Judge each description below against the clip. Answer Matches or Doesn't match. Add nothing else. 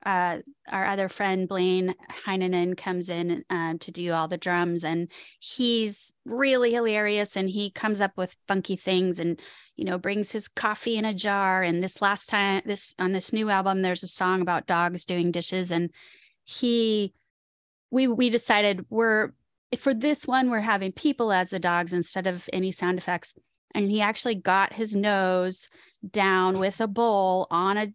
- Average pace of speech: Matches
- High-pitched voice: Matches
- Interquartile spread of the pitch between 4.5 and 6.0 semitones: Doesn't match